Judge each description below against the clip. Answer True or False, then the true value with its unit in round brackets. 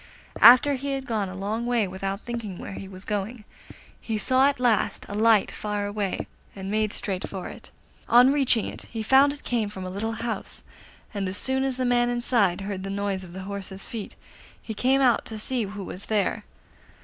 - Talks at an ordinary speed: False (210 wpm)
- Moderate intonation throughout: True (3.7 semitones)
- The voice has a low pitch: False (215 Hz)